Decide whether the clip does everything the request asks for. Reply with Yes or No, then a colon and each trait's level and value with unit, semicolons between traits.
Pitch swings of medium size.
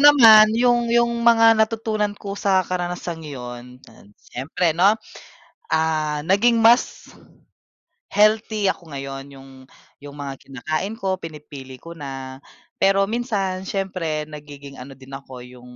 No: wide, 7.4 semitones